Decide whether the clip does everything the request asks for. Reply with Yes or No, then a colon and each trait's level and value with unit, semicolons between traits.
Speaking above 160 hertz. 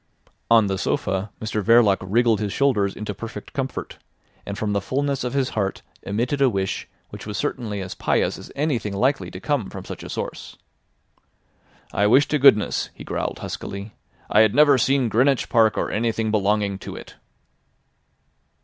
No: low, 110 Hz